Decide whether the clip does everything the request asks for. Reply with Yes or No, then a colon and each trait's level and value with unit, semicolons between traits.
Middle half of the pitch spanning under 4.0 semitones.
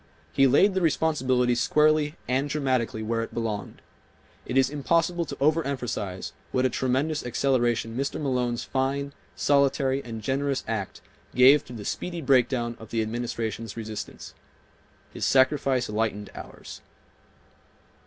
Yes: average, 3.3 semitones